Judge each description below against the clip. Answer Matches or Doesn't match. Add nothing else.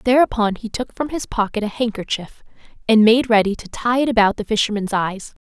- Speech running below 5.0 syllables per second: Doesn't match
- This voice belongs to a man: Doesn't match